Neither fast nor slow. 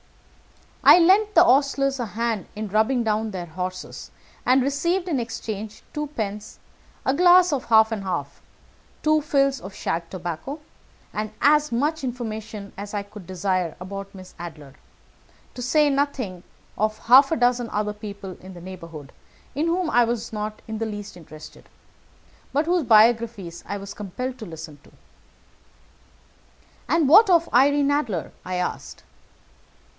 Yes: average, 155 wpm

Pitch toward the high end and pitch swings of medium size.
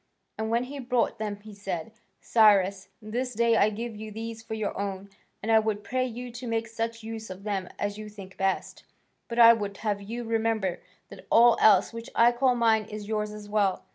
No: high, 220 Hz; narrow, 2.1 semitones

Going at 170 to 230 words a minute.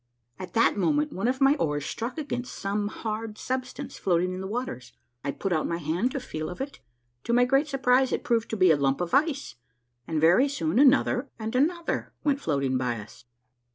Yes: fast, 205 wpm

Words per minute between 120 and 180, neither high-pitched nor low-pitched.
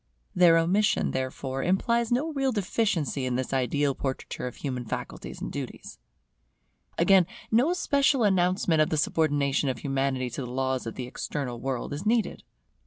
Yes: average, 160 wpm; medium, 150 Hz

